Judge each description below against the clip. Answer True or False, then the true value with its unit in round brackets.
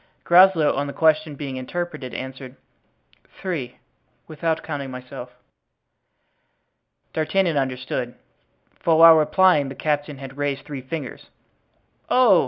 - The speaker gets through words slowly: True (110 wpm)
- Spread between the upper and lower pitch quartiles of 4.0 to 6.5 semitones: False (3.5 semitones)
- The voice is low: False (145 Hz)